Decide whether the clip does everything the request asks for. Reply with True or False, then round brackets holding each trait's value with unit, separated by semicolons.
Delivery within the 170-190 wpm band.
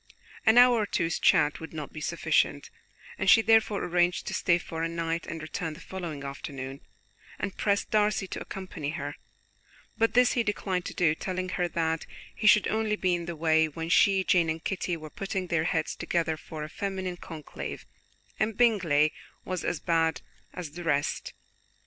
True (185 wpm)